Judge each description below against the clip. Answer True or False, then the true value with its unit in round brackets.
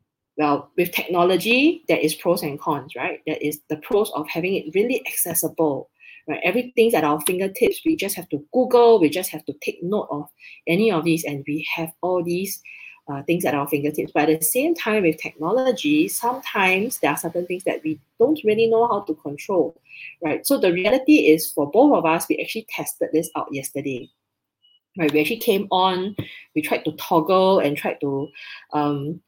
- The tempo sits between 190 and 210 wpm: True (195 wpm)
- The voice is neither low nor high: True (170 Hz)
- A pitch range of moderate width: False (6.5 semitones)